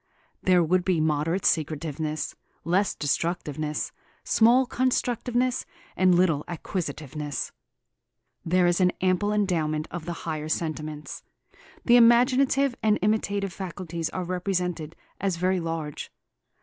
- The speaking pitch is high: No, medium, 175 Hz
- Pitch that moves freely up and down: No, average, 4.1 semitones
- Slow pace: Yes, slow, 110 wpm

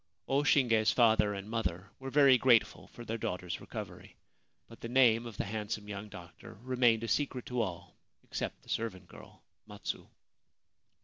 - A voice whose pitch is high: No, low, 115 Hz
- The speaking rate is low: No, average, 165 wpm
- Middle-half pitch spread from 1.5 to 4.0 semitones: Yes, average, 3.5 semitones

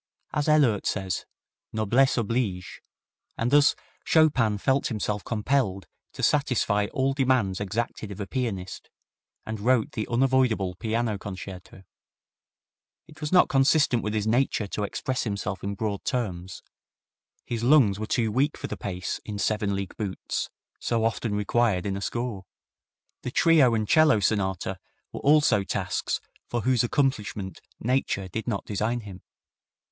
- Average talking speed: Yes, average, 145 wpm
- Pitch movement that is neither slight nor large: Yes, average, 4.4 semitones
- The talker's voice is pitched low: Yes, low, 110 Hz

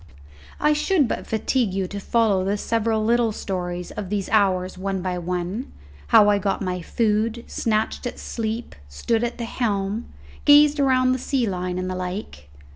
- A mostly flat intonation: No, average, 4.1 semitones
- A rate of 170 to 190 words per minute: Yes, average, 175 wpm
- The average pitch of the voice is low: No, high, 210 Hz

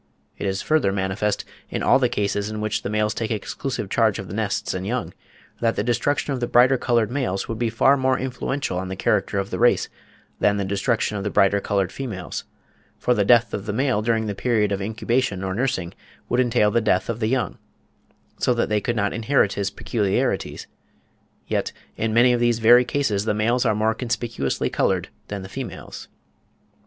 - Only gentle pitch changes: No, average, 3.3 semitones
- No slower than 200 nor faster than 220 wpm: Yes, fast, 205 wpm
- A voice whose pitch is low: Yes, low, 110 Hz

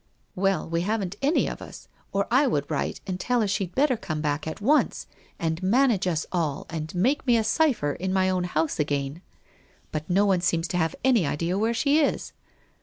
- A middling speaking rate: No, fast, 210 wpm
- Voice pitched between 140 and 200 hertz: Yes, medium, 185 Hz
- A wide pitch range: Yes, wide, 5.9 semitones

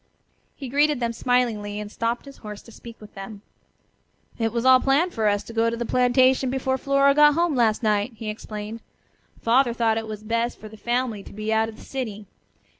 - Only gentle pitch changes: No, average, 3.2 semitones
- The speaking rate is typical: No, fast, 210 wpm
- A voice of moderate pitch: No, high, 230 Hz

